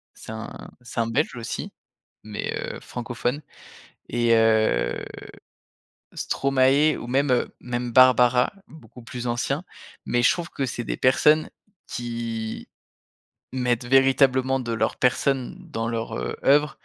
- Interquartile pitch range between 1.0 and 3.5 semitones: Yes, narrow, 2.5 semitones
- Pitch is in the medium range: No, low, 125 Hz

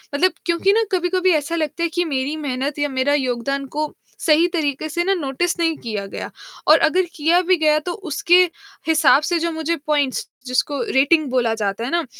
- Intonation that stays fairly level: No, average, 3.7 semitones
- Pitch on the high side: Yes, very high, 310 Hz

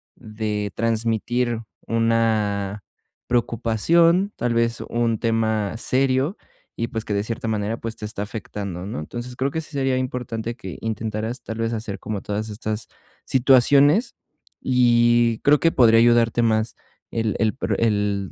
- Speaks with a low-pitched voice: Yes, low, 115 Hz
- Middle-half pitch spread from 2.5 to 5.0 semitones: No, narrow, 2.1 semitones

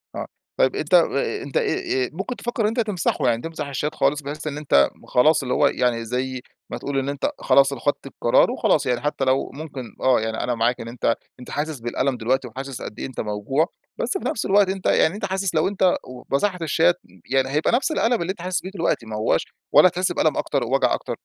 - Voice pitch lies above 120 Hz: Yes, medium, 140 Hz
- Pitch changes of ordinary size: No, wide, 5.8 semitones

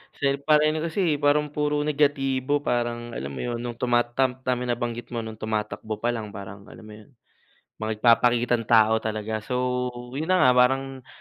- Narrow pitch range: No, average, 3.7 semitones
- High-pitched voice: No, low, 120 Hz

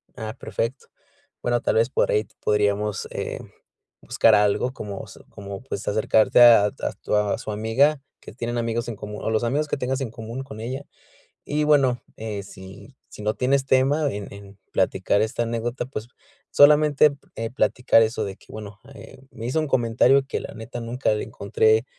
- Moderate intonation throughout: Yes, average, 3.7 semitones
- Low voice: Yes, low, 115 Hz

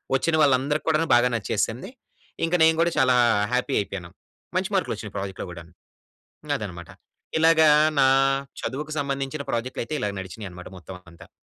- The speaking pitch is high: No, low, 125 Hz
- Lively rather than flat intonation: Yes, wide, 7.6 semitones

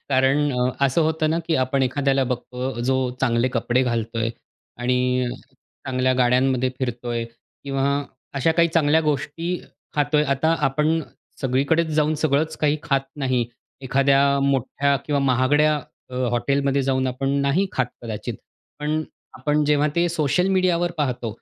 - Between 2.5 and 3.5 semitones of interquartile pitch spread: Yes, average, 2.9 semitones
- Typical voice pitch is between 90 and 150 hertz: Yes, low, 135 Hz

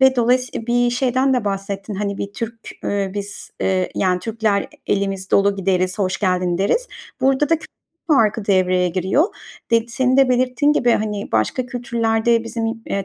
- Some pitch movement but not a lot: Yes, average, 4.0 semitones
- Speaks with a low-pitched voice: No, high, 220 Hz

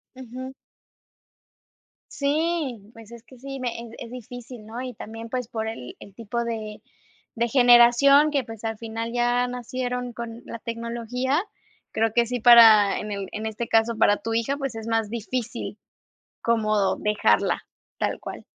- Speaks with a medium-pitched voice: No, high, 235 Hz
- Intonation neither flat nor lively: No, narrow, 1.9 semitones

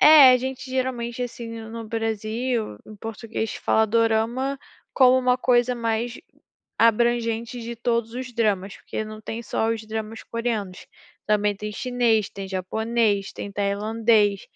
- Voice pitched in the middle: No, high, 225 Hz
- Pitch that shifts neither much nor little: No, narrow, 2.0 semitones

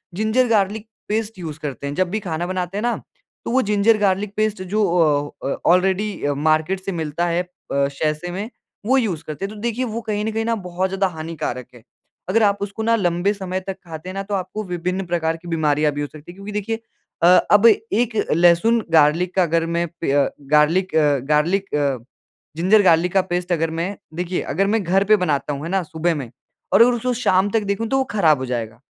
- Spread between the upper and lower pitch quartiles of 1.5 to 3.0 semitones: No, average, 4.4 semitones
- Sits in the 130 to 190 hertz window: Yes, medium, 185 Hz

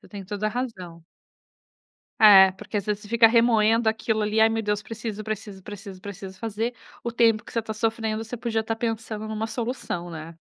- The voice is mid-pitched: No, high, 220 Hz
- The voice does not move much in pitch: Yes, narrow, 1.7 semitones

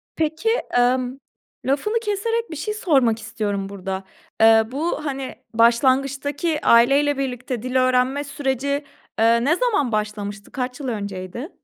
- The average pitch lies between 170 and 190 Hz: No, very high, 260 Hz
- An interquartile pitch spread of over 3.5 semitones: Yes, average, 4.1 semitones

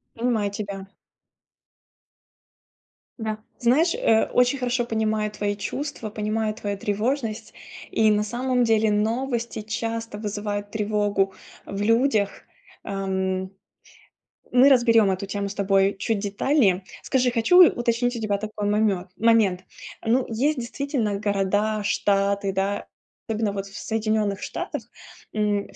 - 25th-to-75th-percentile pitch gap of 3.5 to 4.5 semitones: No, narrow, 2.5 semitones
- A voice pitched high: Yes, high, 215 Hz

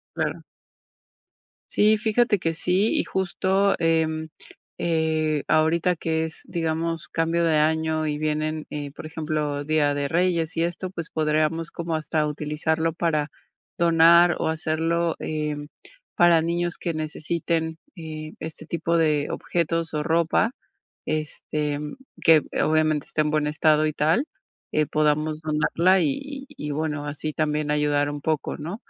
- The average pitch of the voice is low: No, medium, 160 Hz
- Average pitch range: No, narrow, 1.7 semitones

